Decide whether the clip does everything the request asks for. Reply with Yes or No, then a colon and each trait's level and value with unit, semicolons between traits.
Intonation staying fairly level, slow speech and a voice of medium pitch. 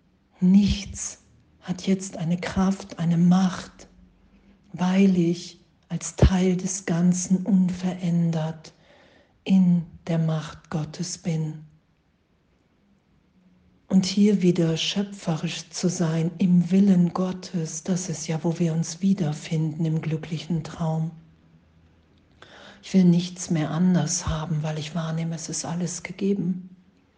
Yes: narrow, 2.3 semitones; slow, 115 wpm; medium, 170 Hz